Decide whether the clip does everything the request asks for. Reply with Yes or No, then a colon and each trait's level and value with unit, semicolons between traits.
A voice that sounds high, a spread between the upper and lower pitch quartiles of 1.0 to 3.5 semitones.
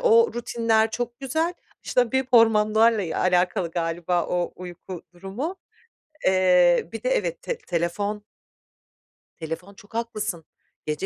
No: high, 205 Hz; average, 4.9 semitones